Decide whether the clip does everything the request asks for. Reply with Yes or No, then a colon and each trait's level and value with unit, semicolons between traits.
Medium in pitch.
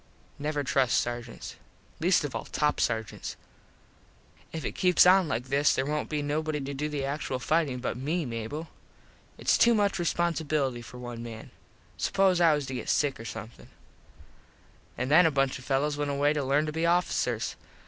Yes: medium, 145 Hz